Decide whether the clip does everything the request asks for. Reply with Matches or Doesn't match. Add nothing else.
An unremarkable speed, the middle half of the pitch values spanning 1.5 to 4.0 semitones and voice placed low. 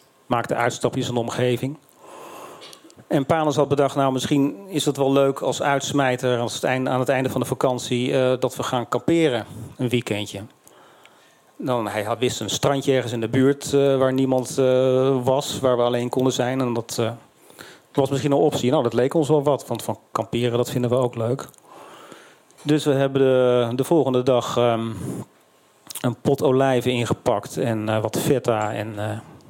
Matches